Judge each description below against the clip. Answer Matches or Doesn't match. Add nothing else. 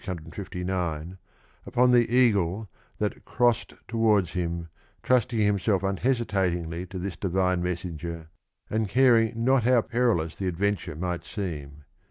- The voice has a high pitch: Doesn't match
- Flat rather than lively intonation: Doesn't match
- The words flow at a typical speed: Doesn't match